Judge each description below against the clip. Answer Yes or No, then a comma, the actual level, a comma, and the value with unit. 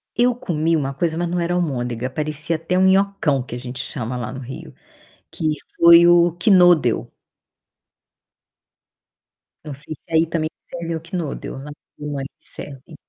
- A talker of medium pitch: Yes, medium, 160 Hz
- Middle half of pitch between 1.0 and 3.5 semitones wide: No, average, 4.1 semitones